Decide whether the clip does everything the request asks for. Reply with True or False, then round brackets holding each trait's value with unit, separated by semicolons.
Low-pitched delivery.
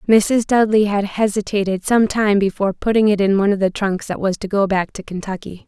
False (200 Hz)